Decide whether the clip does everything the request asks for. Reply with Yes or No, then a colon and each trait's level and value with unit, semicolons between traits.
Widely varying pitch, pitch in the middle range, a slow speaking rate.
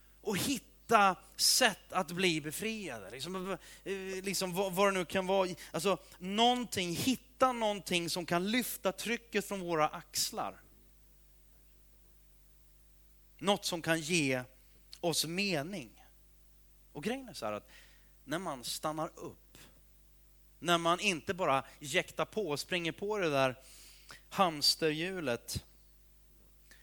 Yes: wide, 6.4 semitones; medium, 175 Hz; slow, 120 wpm